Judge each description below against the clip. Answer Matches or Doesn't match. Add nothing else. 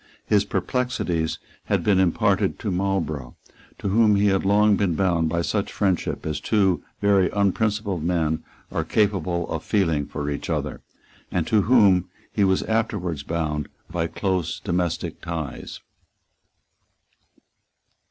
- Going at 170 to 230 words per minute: Doesn't match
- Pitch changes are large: Doesn't match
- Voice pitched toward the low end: Matches